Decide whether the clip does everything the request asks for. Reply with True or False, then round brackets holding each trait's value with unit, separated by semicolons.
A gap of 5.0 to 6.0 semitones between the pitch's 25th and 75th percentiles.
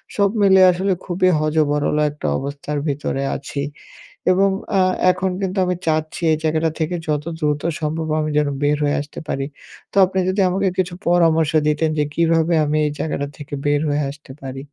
False (3.3 semitones)